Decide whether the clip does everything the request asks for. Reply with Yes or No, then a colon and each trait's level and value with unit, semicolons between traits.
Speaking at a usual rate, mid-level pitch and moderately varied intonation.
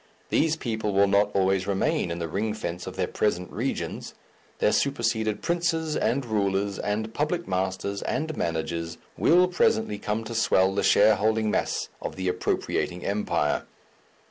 No: average, 150 wpm; low, 105 Hz; average, 3.5 semitones